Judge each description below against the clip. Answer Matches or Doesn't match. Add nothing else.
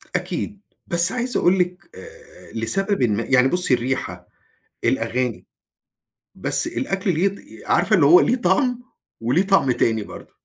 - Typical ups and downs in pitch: Doesn't match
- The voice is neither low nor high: Matches